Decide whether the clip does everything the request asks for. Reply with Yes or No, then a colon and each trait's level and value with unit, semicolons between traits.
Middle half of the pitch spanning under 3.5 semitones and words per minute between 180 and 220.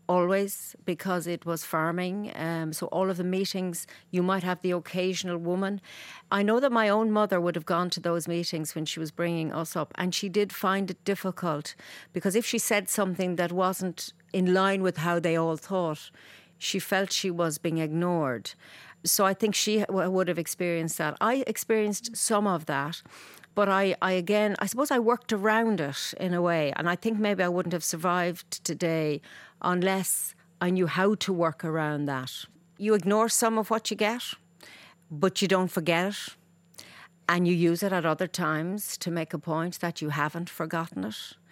Yes: average, 2.8 semitones; average, 190 wpm